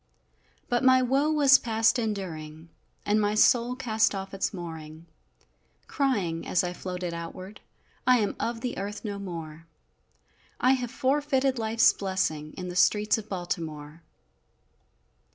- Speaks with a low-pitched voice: No, high, 205 Hz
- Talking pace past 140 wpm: No, slow, 135 wpm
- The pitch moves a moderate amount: No, wide, 5.9 semitones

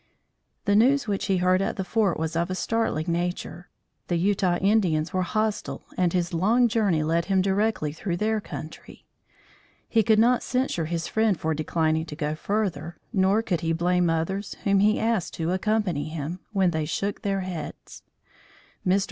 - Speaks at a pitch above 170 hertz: Yes, medium, 185 Hz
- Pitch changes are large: No, average, 4.0 semitones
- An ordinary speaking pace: Yes, average, 175 wpm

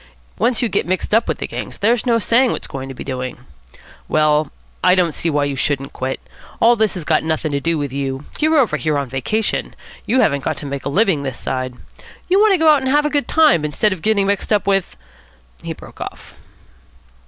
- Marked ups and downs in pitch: Yes, wide, 8.5 semitones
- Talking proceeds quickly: Yes, fast, 235 wpm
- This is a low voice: No, medium, 170 Hz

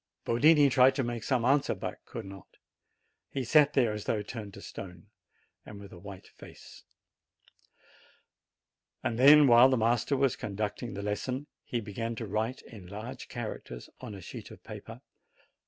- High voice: No, low, 115 Hz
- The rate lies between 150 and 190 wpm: Yes, average, 160 wpm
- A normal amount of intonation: Yes, average, 4.1 semitones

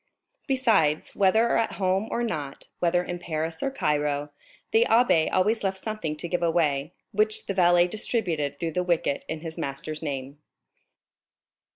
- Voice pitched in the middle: Yes, medium, 175 Hz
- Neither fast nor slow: Yes, average, 155 wpm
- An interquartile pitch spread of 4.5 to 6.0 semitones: Yes, wide, 5.4 semitones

